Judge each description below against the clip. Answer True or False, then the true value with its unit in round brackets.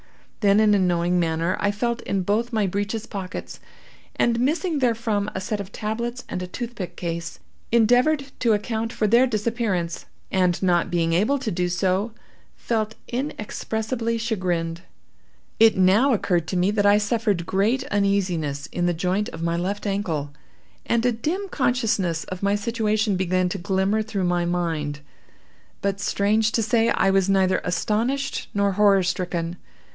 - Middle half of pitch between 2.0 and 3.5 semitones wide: False (4.0 semitones)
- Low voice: False (200 Hz)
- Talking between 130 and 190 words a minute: True (160 wpm)